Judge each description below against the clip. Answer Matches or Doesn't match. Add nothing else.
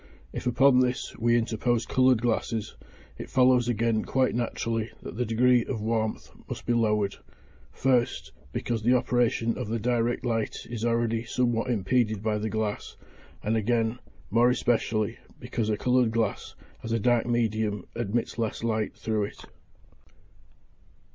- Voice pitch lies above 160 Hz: Doesn't match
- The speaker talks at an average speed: Matches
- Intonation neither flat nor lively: Doesn't match